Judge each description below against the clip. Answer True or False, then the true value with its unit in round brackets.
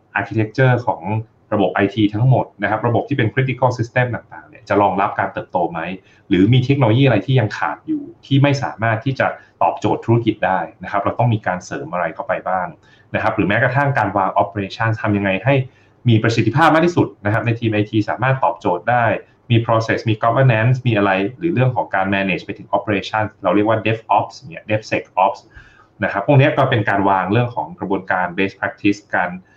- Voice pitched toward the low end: True (110 Hz)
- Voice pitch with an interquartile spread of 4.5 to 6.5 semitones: False (4.0 semitones)